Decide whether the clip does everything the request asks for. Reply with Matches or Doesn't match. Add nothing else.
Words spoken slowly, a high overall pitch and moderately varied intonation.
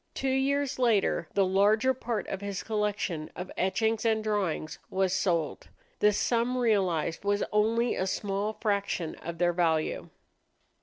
Doesn't match